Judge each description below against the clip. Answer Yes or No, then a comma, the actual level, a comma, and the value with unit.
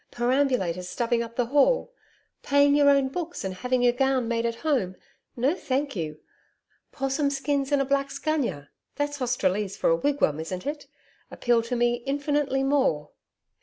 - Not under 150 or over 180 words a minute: Yes, average, 165 wpm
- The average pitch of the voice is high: Yes, very high, 260 Hz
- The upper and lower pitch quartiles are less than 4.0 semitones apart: Yes, average, 3.6 semitones